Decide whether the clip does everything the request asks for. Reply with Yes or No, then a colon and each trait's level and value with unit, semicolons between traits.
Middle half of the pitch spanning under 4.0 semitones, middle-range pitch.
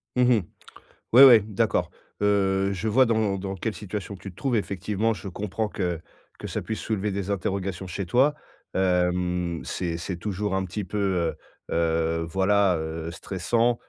No: average, 2.9 semitones; very low, 95 Hz